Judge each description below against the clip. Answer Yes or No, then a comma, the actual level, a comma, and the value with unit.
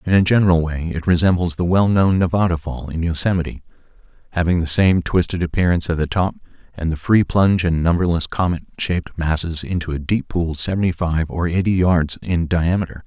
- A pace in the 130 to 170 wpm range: No, average, 185 wpm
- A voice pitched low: Yes, very low, 85 Hz